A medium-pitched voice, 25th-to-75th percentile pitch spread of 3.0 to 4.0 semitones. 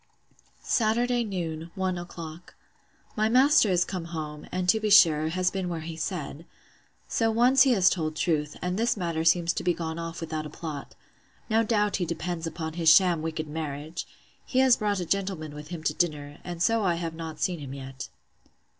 Yes: medium, 170 Hz; average, 3.7 semitones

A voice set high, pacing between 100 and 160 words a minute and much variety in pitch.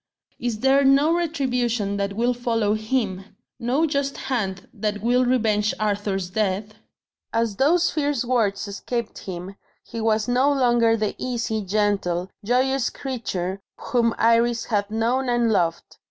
No: high, 230 Hz; average, 140 wpm; average, 3.5 semitones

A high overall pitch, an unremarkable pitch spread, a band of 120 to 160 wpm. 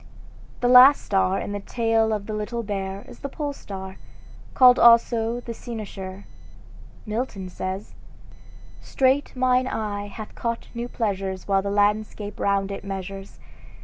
Yes: high, 210 Hz; average, 3.3 semitones; average, 145 wpm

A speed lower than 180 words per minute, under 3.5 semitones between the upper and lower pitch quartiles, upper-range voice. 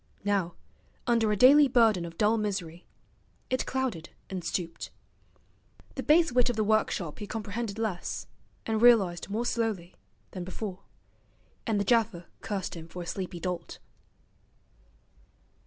No: average, 140 wpm; average, 4.3 semitones; high, 205 Hz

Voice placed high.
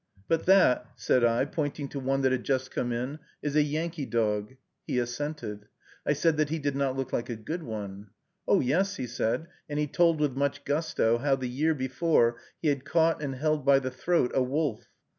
No: low, 135 Hz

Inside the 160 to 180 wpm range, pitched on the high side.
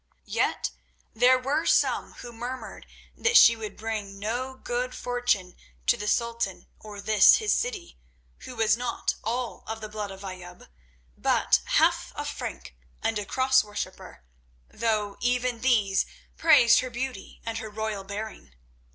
No: average, 150 wpm; high, 225 Hz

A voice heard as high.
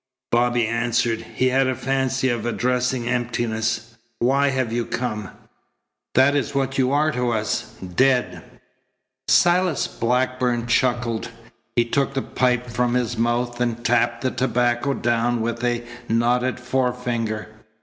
No: low, 120 Hz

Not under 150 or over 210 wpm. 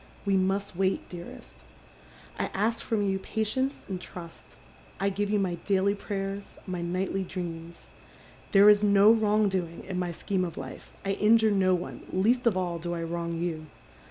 Yes: average, 175 wpm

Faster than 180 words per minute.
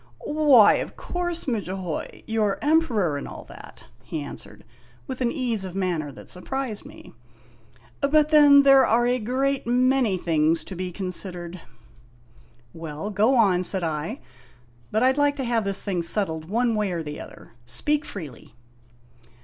No: average, 160 wpm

